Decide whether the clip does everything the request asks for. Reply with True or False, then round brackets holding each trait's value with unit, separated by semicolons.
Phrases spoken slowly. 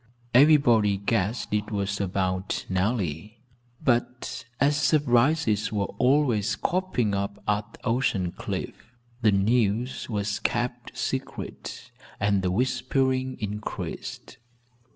True (100 wpm)